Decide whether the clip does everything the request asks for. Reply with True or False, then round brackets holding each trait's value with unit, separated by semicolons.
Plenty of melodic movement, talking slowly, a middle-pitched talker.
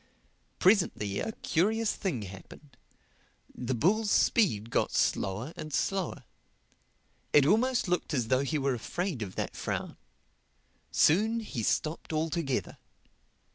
True (7.9 semitones; 120 wpm; 155 Hz)